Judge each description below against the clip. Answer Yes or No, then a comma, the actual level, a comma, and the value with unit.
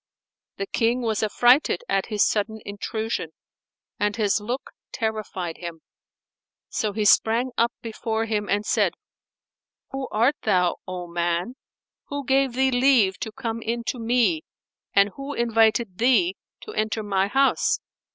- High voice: Yes, high, 220 Hz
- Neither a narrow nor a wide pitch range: Yes, average, 3.3 semitones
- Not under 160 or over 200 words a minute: No, average, 140 wpm